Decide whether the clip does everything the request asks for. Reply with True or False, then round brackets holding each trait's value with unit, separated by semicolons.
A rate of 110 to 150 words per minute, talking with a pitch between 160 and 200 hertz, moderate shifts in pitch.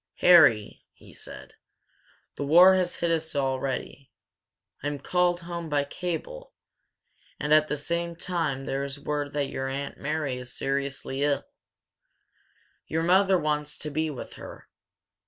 False (140 wpm; 150 Hz; 3.5 semitones)